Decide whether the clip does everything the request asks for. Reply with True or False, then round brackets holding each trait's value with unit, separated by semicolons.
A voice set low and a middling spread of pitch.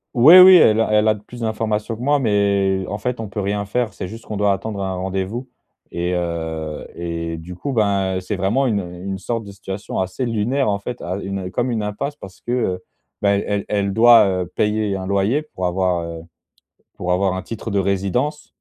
True (100 Hz; 3.2 semitones)